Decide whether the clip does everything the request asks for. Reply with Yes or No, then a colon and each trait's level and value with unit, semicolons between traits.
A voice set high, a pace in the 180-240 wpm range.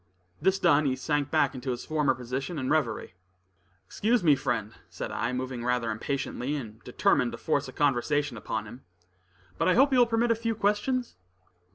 No: medium, 140 Hz; average, 185 wpm